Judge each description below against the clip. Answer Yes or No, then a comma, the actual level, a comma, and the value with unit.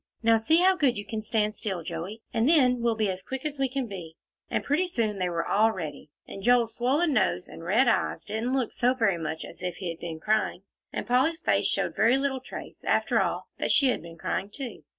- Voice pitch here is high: Yes, high, 225 Hz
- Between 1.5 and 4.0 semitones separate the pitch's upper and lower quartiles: No, wide, 5.5 semitones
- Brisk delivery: Yes, fast, 235 wpm